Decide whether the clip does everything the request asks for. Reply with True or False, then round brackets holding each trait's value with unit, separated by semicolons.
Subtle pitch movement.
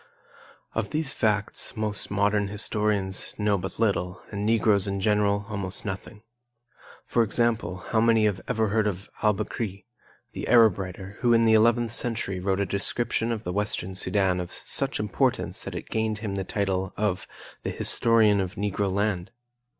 True (2.3 semitones)